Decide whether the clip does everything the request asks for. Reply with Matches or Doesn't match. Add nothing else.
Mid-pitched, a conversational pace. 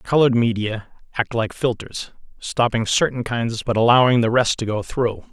Doesn't match